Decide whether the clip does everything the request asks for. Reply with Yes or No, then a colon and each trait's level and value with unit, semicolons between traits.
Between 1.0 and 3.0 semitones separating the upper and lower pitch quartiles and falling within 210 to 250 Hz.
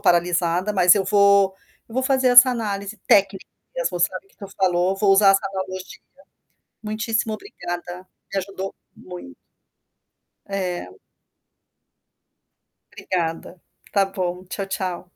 No: narrow, 2.6 semitones; high, 195 Hz